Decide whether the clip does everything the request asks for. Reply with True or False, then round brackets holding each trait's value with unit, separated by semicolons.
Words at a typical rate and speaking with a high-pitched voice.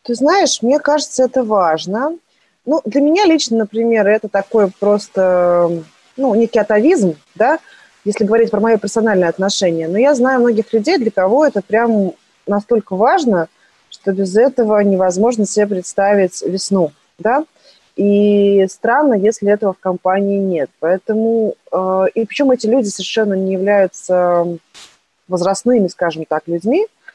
True (135 wpm; 210 Hz)